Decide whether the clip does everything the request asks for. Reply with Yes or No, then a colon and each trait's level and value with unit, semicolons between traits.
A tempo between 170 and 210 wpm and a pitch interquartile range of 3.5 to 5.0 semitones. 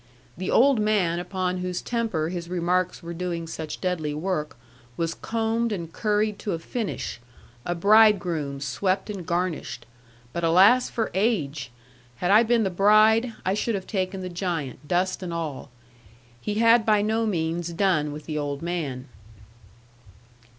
No: average, 155 wpm; average, 4.2 semitones